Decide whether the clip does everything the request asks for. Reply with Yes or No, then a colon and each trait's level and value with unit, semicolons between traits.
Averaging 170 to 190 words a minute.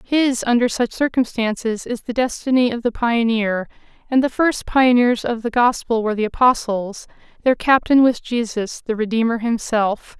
No: average, 155 wpm